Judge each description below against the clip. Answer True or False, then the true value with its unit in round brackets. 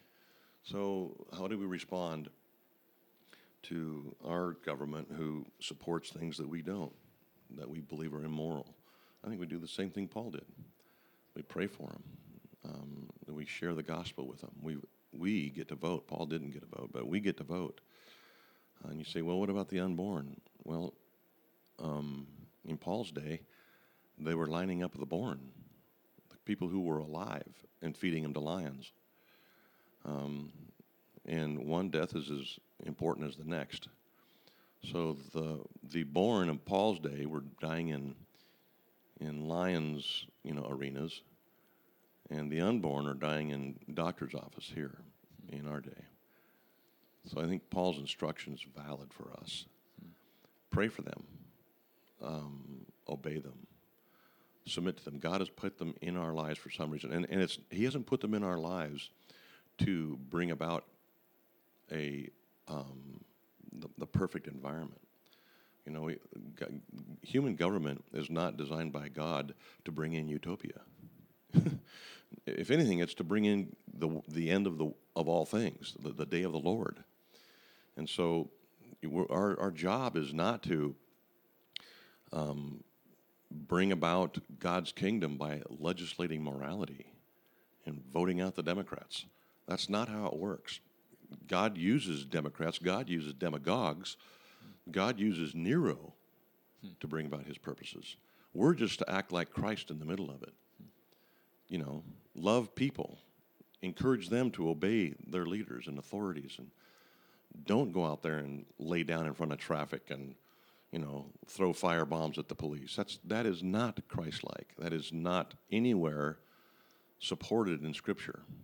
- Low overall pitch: True (80 Hz)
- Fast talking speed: False (150 wpm)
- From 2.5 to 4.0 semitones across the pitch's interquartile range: True (2.9 semitones)